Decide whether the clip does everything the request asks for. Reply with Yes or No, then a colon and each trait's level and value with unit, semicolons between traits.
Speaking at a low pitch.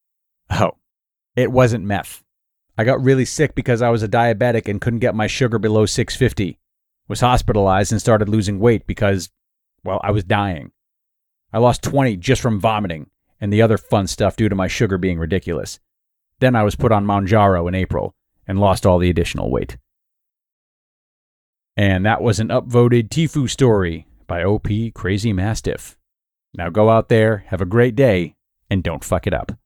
Yes: low, 105 Hz